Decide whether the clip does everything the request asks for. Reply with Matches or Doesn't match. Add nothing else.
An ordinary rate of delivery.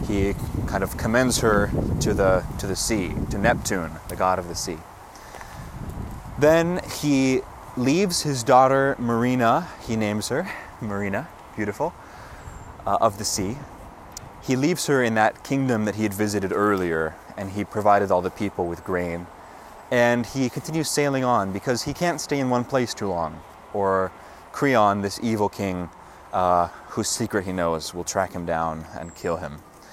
Matches